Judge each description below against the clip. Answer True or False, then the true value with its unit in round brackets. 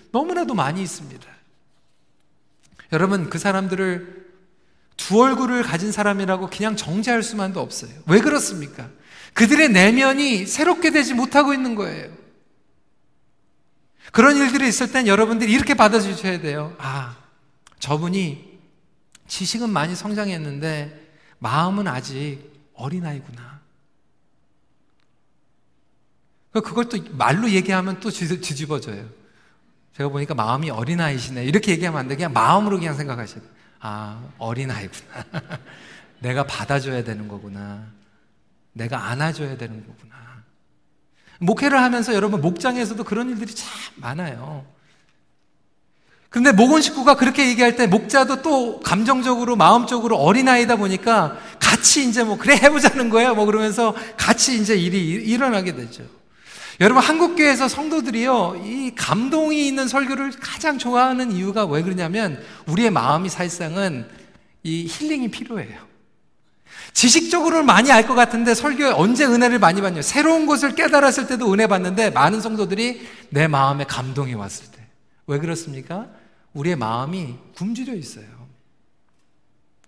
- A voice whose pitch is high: True (195 Hz)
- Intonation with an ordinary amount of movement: False (8.6 semitones)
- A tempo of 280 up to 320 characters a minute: True (310 characters per minute)